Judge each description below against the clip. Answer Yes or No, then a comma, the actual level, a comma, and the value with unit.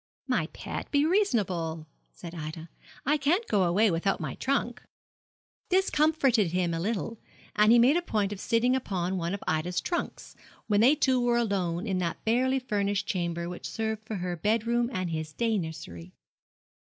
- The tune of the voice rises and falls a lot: Yes, wide, 5.7 semitones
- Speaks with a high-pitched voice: Yes, high, 205 Hz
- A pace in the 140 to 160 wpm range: No, average, 180 wpm